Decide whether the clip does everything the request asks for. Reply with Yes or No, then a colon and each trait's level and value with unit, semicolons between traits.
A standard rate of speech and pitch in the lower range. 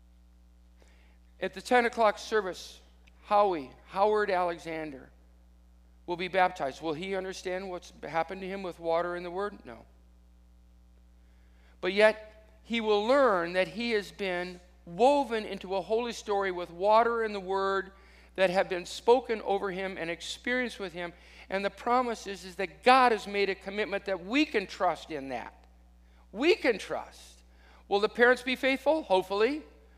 No: average, 160 wpm; high, 190 Hz